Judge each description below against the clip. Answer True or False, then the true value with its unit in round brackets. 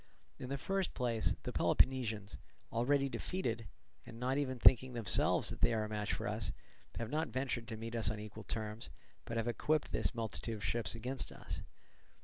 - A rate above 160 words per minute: True (185 wpm)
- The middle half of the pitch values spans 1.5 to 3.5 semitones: True (3.0 semitones)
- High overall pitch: False (115 Hz)